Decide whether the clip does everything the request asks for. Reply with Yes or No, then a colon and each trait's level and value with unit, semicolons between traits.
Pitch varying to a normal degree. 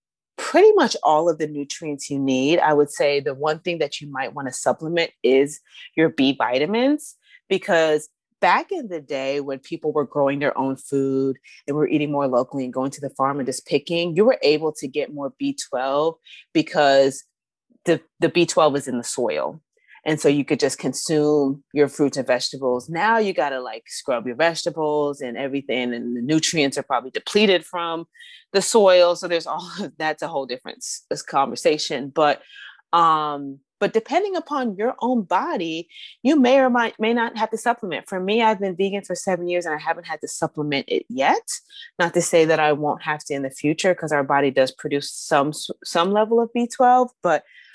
No: wide, 6.3 semitones